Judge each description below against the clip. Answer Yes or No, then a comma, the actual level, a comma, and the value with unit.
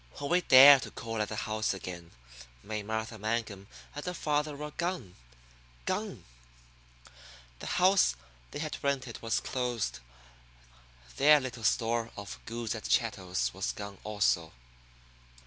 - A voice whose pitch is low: Yes, low, 115 Hz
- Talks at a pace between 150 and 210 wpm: No, slow, 135 wpm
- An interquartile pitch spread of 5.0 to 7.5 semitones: Yes, average, 5.3 semitones